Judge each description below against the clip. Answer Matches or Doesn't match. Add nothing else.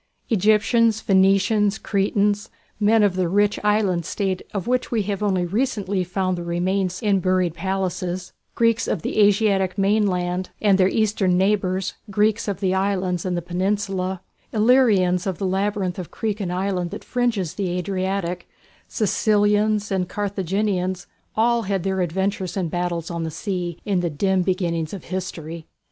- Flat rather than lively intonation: Matches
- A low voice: Doesn't match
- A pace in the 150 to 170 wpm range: Matches